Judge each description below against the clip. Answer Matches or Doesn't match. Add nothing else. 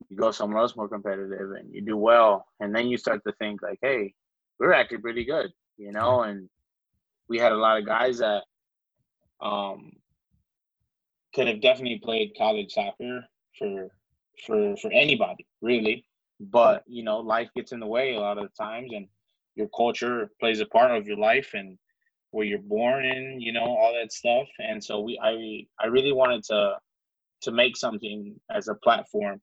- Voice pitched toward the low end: Matches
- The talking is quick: Doesn't match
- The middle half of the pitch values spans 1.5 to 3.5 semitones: Matches